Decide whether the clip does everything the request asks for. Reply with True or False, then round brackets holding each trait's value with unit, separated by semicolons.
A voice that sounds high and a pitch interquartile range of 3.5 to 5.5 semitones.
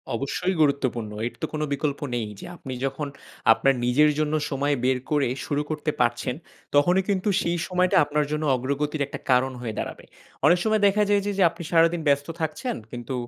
False (145 Hz; 4.2 semitones)